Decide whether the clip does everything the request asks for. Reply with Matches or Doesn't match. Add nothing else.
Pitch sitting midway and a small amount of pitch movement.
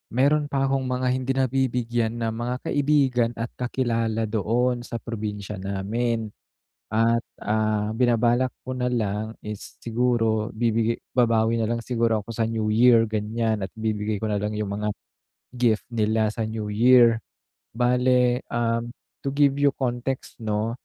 Doesn't match